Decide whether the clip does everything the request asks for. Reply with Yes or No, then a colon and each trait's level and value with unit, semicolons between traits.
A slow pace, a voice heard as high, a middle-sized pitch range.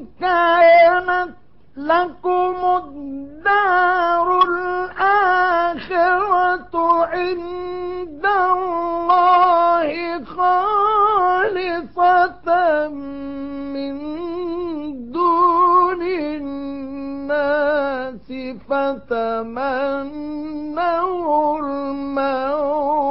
Yes: slow, 30 wpm; very high, 340 Hz; average, 4.1 semitones